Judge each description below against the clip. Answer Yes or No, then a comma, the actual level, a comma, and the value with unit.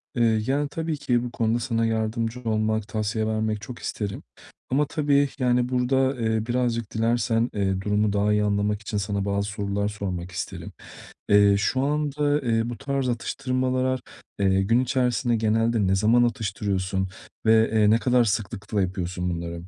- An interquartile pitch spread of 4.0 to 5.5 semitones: No, average, 3.4 semitones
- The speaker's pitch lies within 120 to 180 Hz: No, low, 110 Hz